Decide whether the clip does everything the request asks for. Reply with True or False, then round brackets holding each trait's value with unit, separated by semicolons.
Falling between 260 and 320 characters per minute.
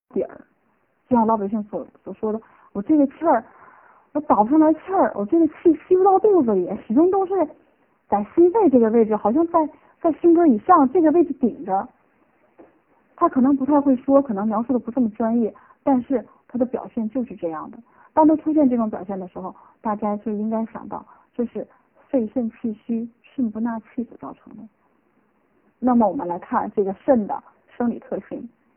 True (275 characters per minute)